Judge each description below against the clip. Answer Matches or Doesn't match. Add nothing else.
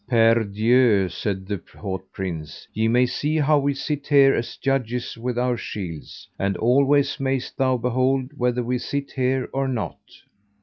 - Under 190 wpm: Matches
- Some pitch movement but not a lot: Matches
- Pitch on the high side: Doesn't match